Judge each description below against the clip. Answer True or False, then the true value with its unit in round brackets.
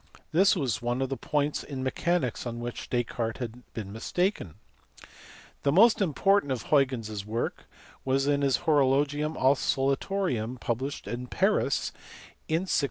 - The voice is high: False (135 Hz)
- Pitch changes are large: False (3.8 semitones)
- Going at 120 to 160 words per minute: True (145 wpm)